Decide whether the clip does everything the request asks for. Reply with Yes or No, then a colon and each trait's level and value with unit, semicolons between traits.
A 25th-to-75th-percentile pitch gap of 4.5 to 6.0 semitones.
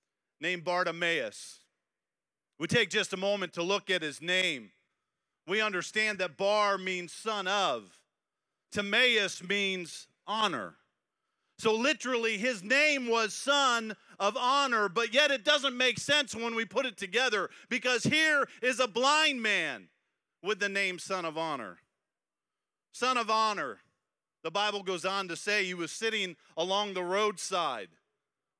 Yes: average, 4.9 semitones